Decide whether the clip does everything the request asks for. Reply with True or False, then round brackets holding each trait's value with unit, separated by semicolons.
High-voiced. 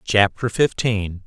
False (105 Hz)